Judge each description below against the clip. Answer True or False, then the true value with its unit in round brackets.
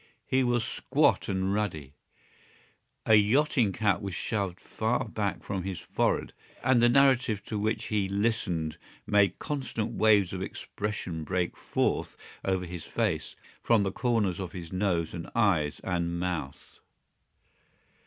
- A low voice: True (100 Hz)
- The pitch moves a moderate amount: True (3.7 semitones)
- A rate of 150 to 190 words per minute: False (140 wpm)